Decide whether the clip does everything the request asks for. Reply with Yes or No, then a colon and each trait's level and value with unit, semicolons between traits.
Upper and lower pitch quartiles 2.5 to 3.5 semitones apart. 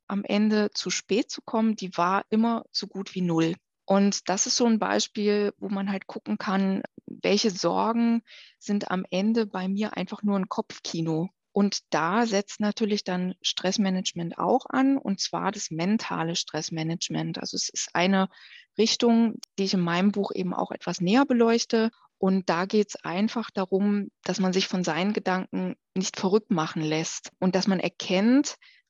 Yes: average, 3.2 semitones